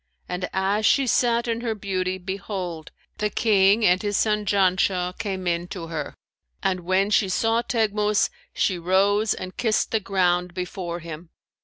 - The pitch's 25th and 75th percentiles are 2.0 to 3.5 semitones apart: Yes, average, 2.8 semitones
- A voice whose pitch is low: No, high, 190 Hz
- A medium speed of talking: Yes, average, 160 wpm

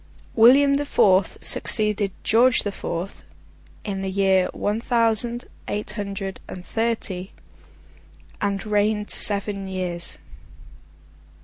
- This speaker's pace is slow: Yes, slow, 105 wpm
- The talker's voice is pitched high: Yes, high, 205 Hz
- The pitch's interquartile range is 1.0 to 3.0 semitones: Yes, narrow, 2.6 semitones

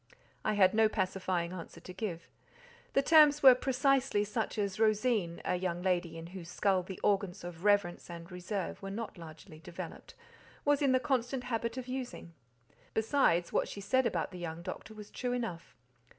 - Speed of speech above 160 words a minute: Yes, average, 170 wpm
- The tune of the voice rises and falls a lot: Yes, wide, 5.9 semitones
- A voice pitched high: Yes, high, 205 Hz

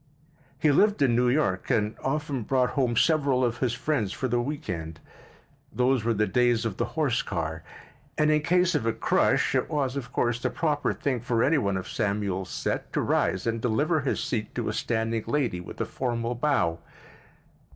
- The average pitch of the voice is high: No, low, 120 Hz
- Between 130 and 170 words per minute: No, average, 195 wpm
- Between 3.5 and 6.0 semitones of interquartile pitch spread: Yes, average, 4.6 semitones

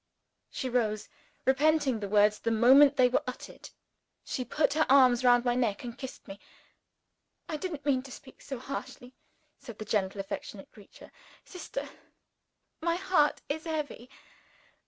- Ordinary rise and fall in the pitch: Yes, average, 4.1 semitones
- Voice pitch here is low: No, very high, 255 Hz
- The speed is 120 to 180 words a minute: Yes, average, 150 wpm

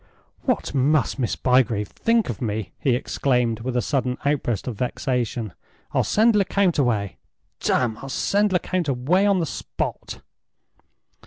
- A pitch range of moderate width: No, wide, 6.1 semitones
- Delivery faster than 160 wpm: No, average, 145 wpm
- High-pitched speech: No, low, 130 Hz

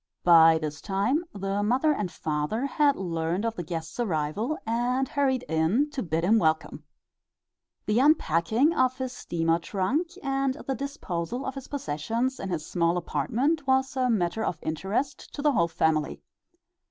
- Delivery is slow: No, average, 160 wpm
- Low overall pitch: No, high, 210 Hz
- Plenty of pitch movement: Yes, wide, 8.1 semitones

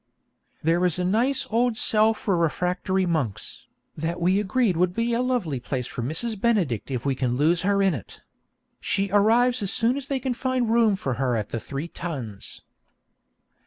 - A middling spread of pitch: No, wide, 7.5 semitones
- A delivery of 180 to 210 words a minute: Yes, average, 185 wpm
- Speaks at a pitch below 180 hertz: No, medium, 185 Hz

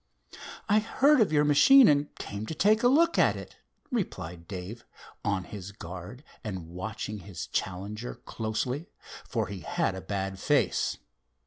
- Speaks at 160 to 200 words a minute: No, average, 150 wpm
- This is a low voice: Yes, low, 110 Hz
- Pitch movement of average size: No, wide, 8.6 semitones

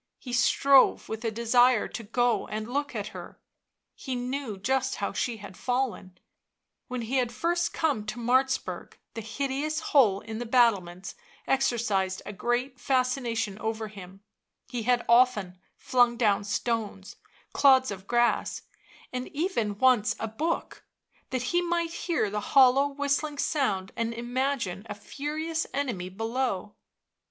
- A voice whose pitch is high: Yes, high, 240 Hz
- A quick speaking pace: No, average, 140 wpm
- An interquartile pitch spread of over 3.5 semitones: Yes, average, 4.1 semitones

